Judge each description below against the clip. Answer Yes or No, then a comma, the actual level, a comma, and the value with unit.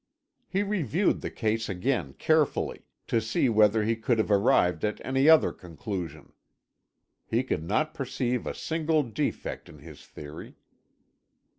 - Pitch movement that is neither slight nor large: No, wide, 7.0 semitones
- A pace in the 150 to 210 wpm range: No, average, 140 wpm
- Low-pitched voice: Yes, low, 115 Hz